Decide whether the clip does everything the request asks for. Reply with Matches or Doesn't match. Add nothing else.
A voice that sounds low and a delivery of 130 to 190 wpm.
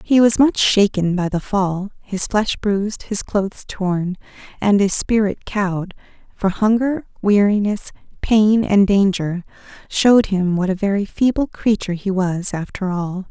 Doesn't match